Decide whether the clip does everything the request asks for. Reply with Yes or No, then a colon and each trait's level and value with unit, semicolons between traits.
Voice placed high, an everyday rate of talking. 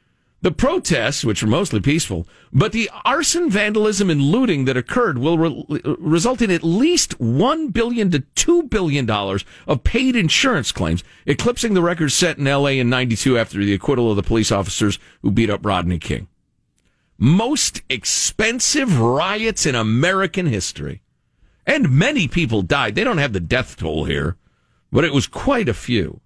No: medium, 140 Hz; average, 170 wpm